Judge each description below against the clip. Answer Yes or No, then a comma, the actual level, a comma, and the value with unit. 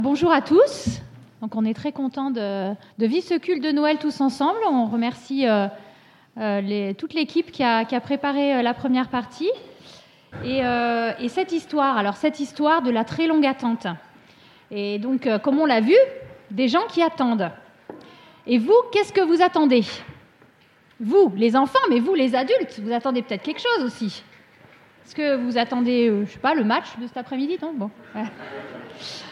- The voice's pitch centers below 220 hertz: No, very high, 260 Hz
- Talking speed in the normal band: Yes, average, 180 wpm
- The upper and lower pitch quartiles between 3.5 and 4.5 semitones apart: No, average, 5.1 semitones